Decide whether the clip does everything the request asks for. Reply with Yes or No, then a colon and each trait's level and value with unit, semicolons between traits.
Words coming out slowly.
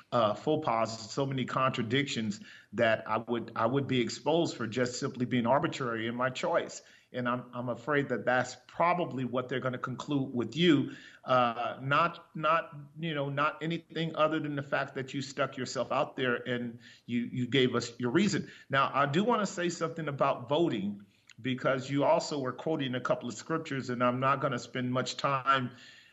No: average, 195 wpm